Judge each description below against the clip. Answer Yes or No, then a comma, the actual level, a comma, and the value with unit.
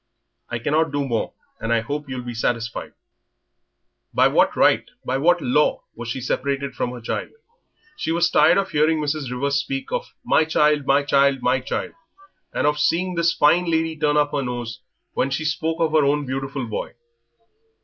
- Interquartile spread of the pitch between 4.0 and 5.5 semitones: No, average, 3.5 semitones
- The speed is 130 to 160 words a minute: No, average, 185 wpm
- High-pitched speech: No, medium, 140 Hz